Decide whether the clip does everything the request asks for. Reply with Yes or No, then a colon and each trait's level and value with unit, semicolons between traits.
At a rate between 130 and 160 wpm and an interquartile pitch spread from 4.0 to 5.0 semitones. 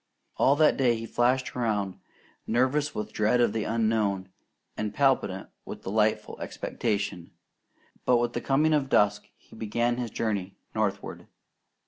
No: average, 140 wpm; average, 3.3 semitones